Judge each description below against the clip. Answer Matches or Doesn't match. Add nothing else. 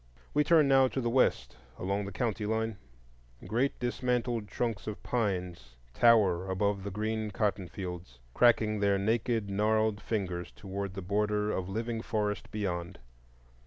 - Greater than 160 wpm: Doesn't match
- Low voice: Matches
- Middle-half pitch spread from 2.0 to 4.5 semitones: Matches